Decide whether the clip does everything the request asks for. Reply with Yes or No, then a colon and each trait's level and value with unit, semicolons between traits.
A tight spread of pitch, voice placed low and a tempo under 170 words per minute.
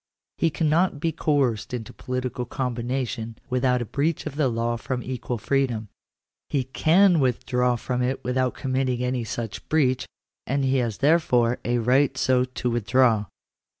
Yes: narrow, 2.1 semitones; low, 125 Hz; average, 150 wpm